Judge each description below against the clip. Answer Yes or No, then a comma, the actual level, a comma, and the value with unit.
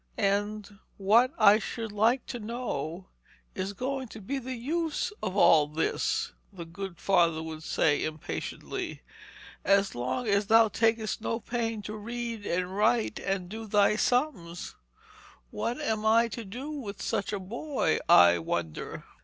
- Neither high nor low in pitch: No, high, 210 Hz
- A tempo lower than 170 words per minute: Yes, average, 150 wpm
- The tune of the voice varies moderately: Yes, average, 3.9 semitones